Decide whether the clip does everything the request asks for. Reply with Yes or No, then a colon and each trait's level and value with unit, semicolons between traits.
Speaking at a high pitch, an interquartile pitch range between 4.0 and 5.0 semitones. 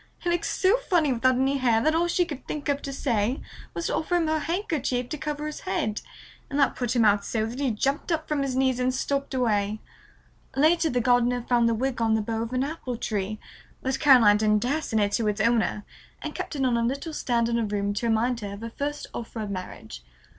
Yes: very high, 250 Hz; average, 4.6 semitones